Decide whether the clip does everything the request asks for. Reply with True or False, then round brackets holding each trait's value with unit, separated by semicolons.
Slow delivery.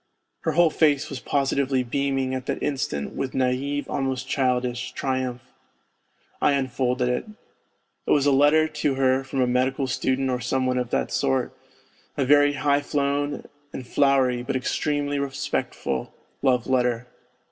False (150 wpm)